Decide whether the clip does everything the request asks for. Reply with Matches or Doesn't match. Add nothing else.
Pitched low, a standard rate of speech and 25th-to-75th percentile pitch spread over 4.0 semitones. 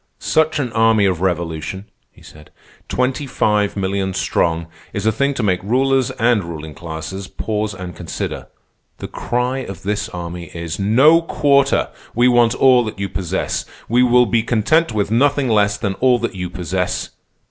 Matches